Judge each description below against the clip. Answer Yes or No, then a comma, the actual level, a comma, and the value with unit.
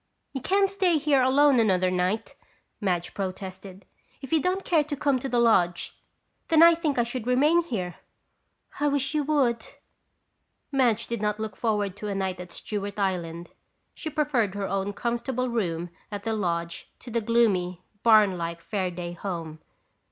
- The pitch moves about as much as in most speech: No, wide, 6.5 semitones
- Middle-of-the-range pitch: No, high, 220 Hz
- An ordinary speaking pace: Yes, average, 165 wpm